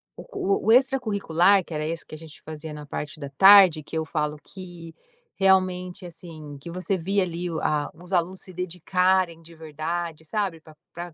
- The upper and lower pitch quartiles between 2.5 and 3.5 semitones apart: Yes, average, 2.9 semitones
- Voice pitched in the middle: Yes, medium, 170 Hz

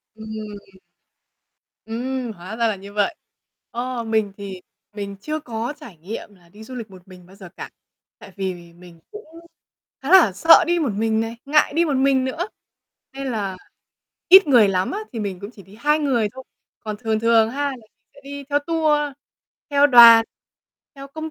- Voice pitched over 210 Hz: Yes, high, 225 Hz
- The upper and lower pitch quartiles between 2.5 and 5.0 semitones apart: No, wide, 5.5 semitones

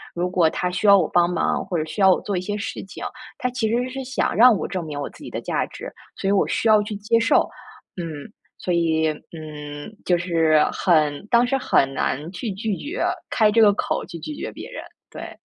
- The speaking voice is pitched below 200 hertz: Yes, medium, 185 Hz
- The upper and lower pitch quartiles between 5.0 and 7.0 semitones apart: Yes, average, 5.3 semitones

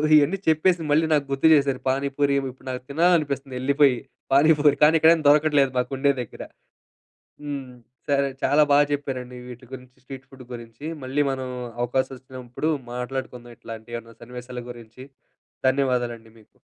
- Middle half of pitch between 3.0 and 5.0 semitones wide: No, narrow, 2.5 semitones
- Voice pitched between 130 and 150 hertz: Yes, low, 135 Hz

